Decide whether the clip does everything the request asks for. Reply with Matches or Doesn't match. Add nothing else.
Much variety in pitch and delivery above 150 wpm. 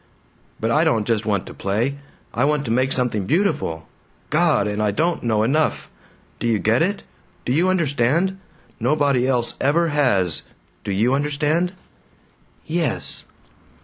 Doesn't match